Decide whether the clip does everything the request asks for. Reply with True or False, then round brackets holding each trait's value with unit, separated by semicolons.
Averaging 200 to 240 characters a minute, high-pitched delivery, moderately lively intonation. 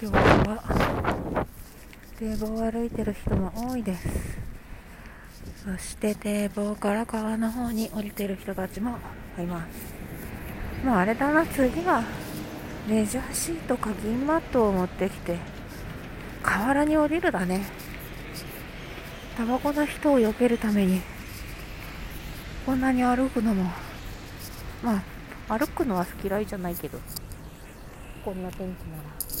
True (235 characters per minute; 215 Hz; 4.7 semitones)